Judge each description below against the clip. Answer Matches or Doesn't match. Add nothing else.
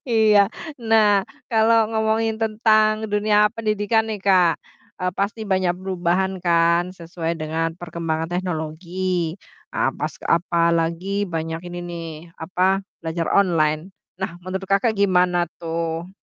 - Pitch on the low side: Doesn't match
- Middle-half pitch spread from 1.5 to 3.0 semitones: Doesn't match